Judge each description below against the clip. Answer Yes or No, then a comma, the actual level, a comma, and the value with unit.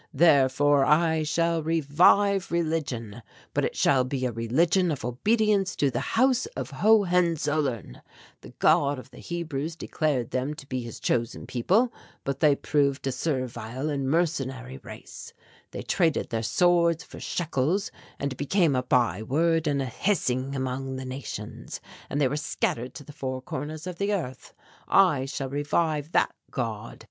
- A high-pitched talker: No, medium, 145 Hz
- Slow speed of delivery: No, average, 155 wpm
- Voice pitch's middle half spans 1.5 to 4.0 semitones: No, average, 4.5 semitones